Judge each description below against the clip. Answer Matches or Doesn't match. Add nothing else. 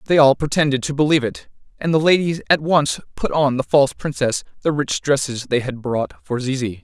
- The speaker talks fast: Matches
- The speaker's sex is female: Doesn't match